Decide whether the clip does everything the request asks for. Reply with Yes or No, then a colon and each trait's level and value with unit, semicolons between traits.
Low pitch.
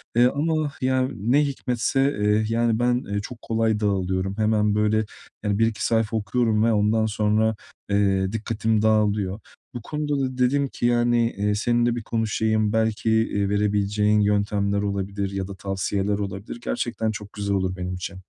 Yes: low, 110 Hz